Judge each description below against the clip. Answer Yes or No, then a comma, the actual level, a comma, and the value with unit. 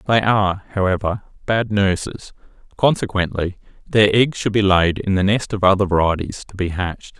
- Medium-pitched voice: No, low, 100 Hz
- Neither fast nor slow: Yes, average, 165 wpm